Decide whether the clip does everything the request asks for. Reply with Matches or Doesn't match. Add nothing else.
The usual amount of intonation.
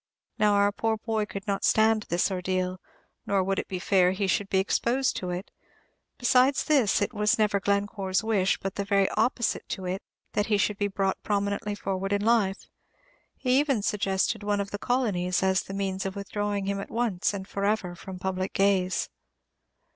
Doesn't match